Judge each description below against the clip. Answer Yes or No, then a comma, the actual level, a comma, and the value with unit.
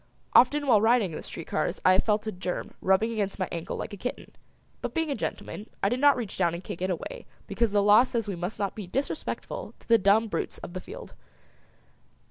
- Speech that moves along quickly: Yes, fast, 235 wpm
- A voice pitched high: Yes, high, 210 Hz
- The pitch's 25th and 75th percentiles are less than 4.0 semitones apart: No, average, 4.3 semitones